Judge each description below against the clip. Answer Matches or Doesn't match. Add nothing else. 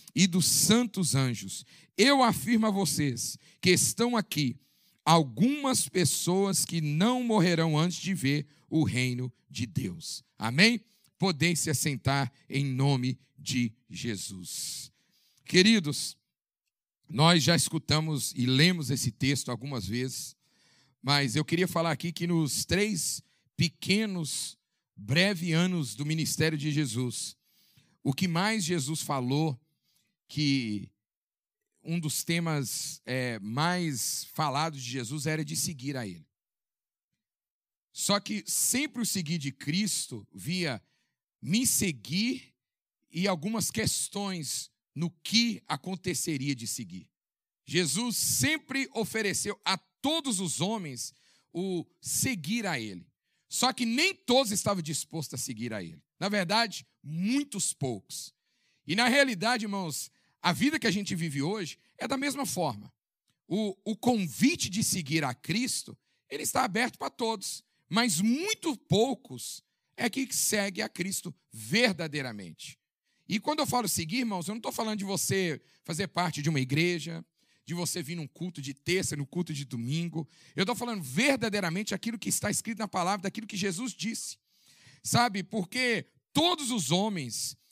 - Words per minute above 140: Doesn't match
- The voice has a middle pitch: Matches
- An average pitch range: Doesn't match